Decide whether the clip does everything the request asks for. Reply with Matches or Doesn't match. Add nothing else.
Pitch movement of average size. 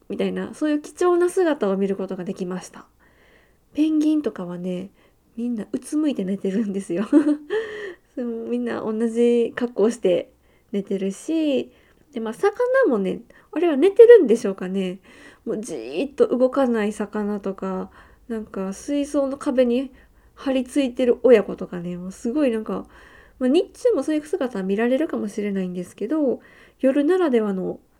Doesn't match